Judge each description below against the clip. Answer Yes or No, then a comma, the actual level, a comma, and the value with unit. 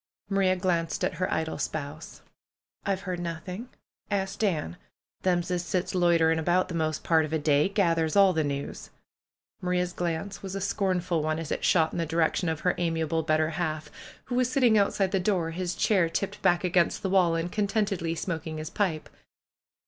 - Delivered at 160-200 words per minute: Yes, average, 195 wpm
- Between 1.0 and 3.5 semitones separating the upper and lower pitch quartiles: Yes, average, 2.9 semitones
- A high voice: No, medium, 175 Hz